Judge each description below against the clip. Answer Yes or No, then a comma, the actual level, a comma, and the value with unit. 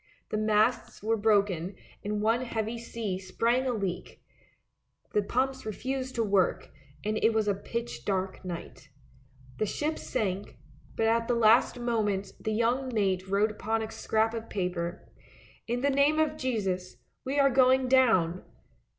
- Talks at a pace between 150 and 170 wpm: Yes, average, 160 wpm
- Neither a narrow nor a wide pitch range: Yes, average, 3.7 semitones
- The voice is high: Yes, high, 220 Hz